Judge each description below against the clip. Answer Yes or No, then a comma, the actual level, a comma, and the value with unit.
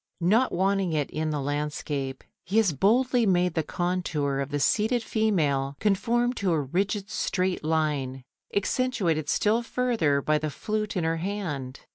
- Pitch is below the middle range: No, medium, 175 Hz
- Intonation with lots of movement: Yes, wide, 6.2 semitones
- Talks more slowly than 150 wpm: No, average, 155 wpm